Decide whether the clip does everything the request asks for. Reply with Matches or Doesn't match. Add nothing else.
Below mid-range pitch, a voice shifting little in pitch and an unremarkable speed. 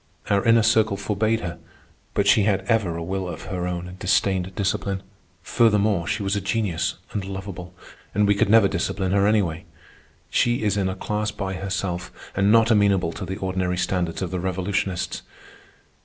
Matches